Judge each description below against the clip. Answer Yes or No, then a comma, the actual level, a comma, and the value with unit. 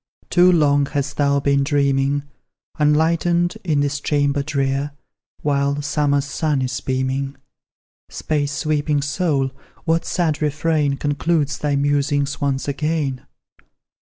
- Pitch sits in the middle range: Yes, medium, 145 Hz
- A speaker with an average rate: No, slow, 115 wpm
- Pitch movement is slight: Yes, narrow, 1.5 semitones